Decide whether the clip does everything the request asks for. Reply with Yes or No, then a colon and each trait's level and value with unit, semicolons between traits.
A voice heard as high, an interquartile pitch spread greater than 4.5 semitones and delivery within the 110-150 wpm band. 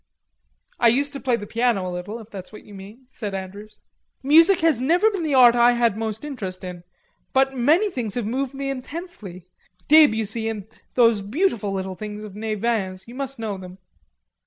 No: high, 230 Hz; average, 4.9 semitones; average, 185 wpm